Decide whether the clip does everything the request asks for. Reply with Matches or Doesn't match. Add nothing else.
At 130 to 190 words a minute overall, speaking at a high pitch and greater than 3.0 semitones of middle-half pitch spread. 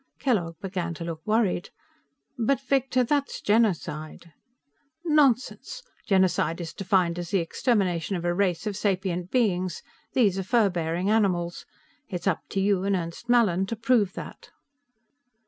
Matches